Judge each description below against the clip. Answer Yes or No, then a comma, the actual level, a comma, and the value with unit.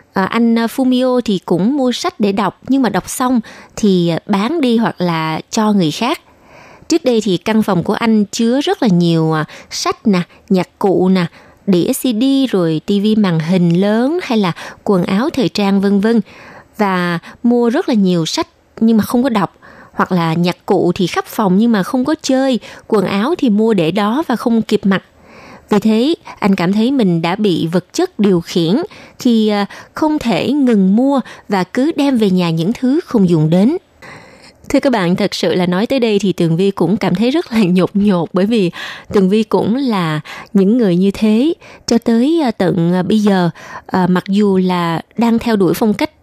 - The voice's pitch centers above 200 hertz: Yes, high, 210 Hz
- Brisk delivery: No, average, 200 wpm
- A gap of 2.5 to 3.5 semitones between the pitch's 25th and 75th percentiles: No, average, 4.8 semitones